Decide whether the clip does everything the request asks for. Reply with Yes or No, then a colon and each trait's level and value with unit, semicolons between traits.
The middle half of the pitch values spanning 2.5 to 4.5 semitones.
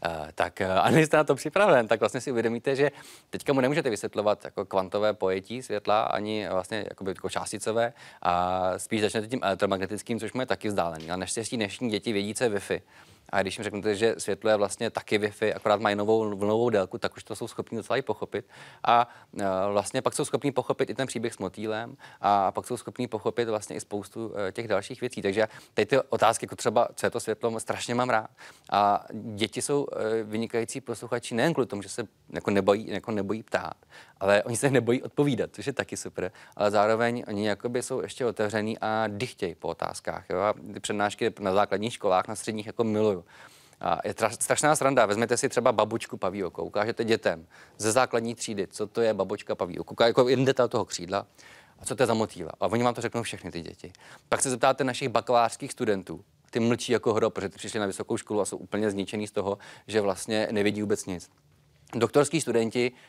Yes: average, 2.9 semitones